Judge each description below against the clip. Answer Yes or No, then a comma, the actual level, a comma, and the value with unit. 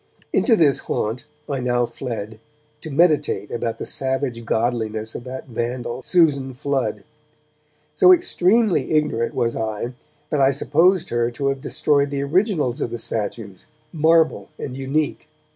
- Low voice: Yes, low, 130 Hz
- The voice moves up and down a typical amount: Yes, average, 4.5 semitones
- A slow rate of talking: No, average, 145 wpm